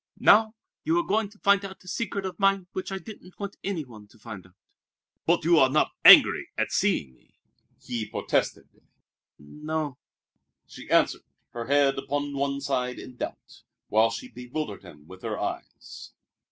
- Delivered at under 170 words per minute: No, average, 180 wpm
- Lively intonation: Yes, wide, 8.3 semitones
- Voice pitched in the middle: Yes, medium, 145 Hz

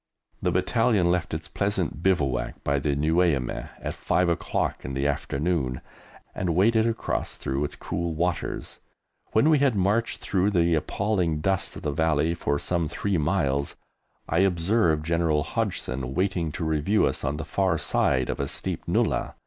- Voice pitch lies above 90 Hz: No, very low, 85 Hz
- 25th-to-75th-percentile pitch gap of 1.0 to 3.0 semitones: No, average, 4.5 semitones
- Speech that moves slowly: No, average, 165 wpm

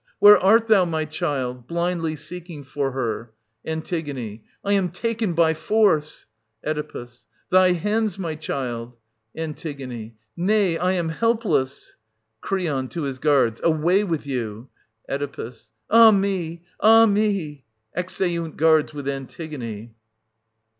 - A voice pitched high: No, medium, 160 Hz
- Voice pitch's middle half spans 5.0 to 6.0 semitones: Yes, average, 5.3 semitones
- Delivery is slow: Yes, slow, 125 wpm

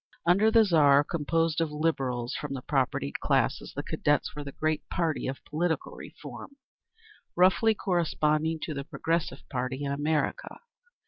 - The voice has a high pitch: No, medium, 155 Hz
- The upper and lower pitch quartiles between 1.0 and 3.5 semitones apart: Yes, average, 3.1 semitones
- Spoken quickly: No, average, 145 wpm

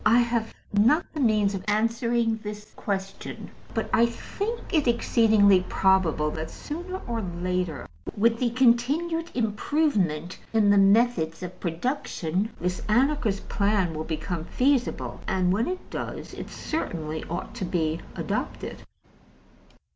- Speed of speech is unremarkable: No, slow, 130 wpm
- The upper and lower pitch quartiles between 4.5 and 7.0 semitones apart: Yes, average, 4.9 semitones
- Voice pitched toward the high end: Yes, high, 210 Hz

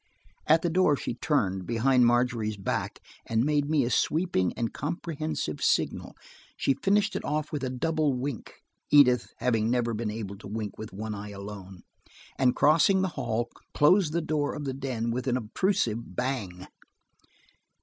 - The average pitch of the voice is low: Yes, low, 125 Hz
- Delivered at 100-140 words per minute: No, average, 165 wpm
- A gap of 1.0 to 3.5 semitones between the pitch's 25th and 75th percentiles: No, wide, 5.5 semitones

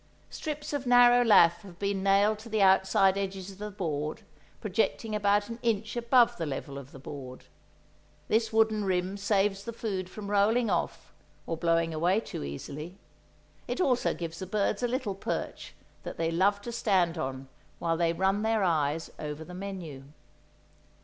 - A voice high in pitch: Yes, high, 195 Hz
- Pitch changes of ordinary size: Yes, average, 4.6 semitones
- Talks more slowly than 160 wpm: No, average, 170 wpm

